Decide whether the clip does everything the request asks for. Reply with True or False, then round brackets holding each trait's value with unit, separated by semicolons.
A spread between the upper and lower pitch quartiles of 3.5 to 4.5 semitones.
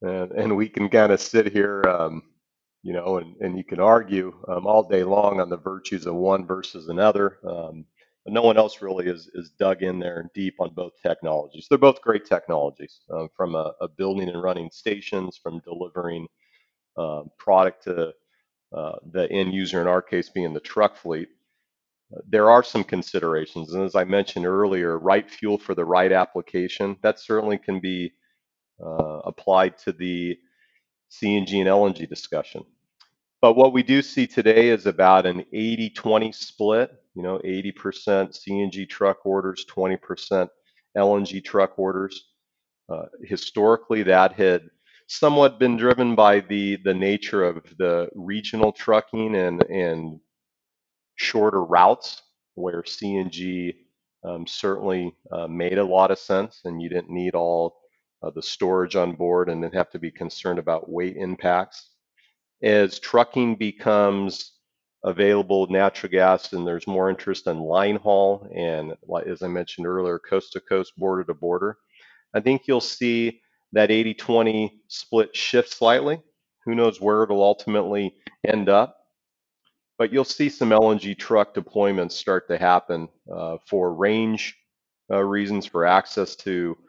False (3.0 semitones)